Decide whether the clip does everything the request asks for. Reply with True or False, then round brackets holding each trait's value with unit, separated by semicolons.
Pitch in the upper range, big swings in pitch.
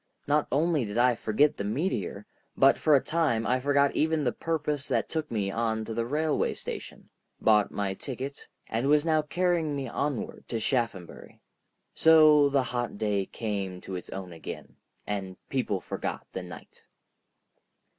False (125 Hz; 6.0 semitones)